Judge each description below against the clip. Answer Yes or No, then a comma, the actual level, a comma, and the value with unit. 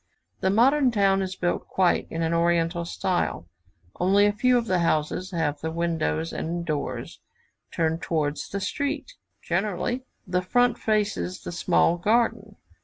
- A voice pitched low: No, medium, 180 Hz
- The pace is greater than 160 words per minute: No, average, 150 wpm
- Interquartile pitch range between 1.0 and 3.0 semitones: No, average, 4.0 semitones